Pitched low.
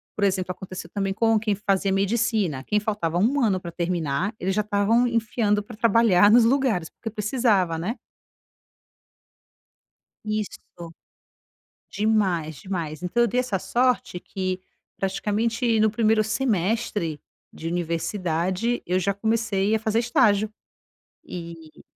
No: high, 205 Hz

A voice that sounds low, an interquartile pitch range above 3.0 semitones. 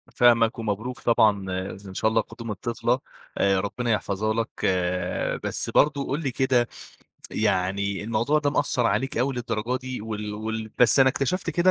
Yes: low, 115 Hz; average, 3.4 semitones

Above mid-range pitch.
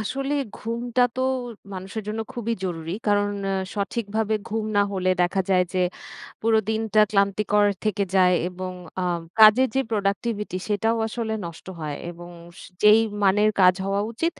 Yes: high, 210 Hz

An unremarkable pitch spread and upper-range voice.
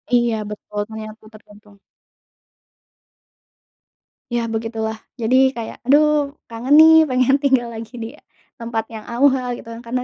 Yes: average, 3.0 semitones; high, 235 Hz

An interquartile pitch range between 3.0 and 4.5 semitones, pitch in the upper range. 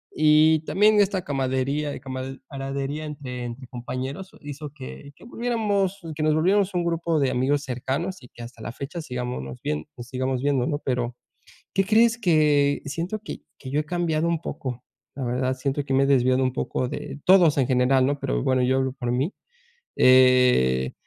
No: average, 3.7 semitones; medium, 140 Hz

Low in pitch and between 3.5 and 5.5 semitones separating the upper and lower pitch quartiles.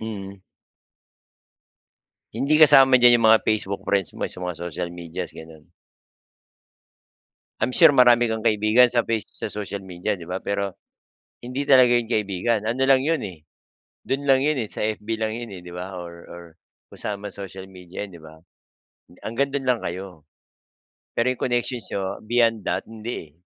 Yes: low, 110 Hz; average, 4.5 semitones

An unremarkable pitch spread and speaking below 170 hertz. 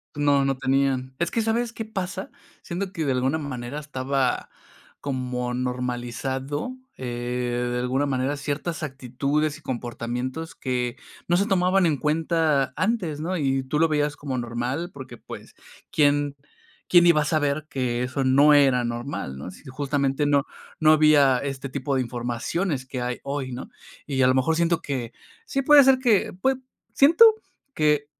Yes: average, 3.6 semitones; medium, 140 Hz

